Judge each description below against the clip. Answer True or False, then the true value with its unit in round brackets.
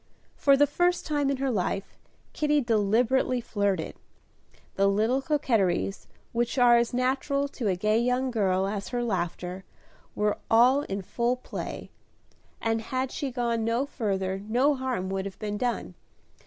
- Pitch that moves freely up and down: False (4.6 semitones)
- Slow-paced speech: False (155 wpm)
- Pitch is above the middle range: True (235 Hz)